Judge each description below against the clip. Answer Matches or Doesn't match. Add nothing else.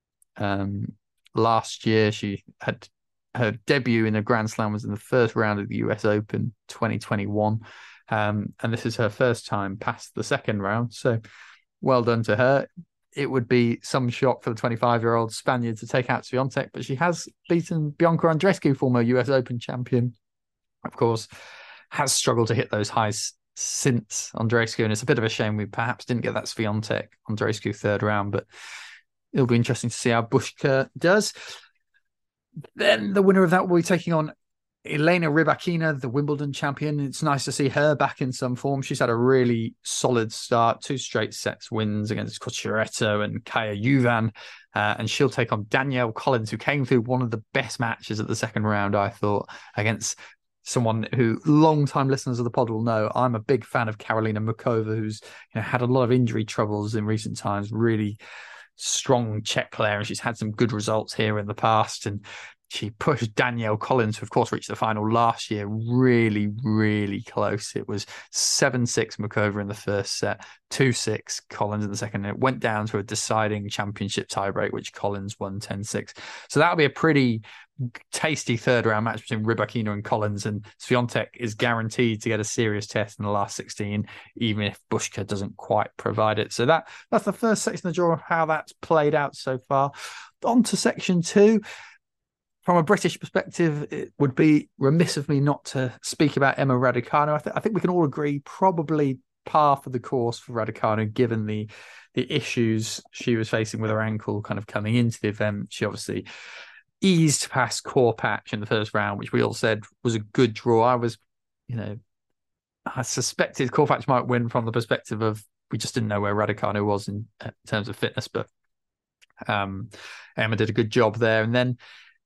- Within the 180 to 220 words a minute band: Matches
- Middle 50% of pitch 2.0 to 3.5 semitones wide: Doesn't match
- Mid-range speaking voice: Doesn't match